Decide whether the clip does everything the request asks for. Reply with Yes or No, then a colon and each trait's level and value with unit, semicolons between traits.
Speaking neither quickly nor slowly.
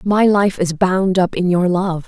No: fast, 230 wpm